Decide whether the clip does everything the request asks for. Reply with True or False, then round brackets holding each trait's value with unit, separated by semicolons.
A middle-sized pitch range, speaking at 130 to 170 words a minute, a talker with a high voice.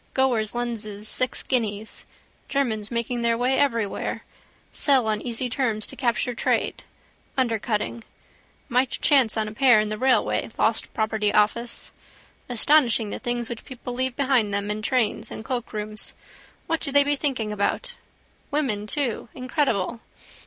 True (3.4 semitones; 140 wpm; 235 Hz)